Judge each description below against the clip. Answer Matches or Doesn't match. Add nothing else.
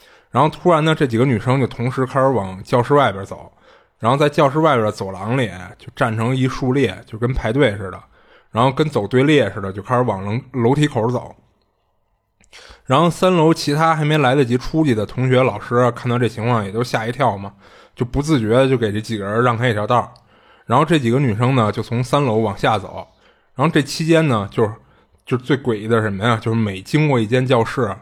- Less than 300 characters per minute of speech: Doesn't match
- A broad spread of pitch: Doesn't match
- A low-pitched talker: Matches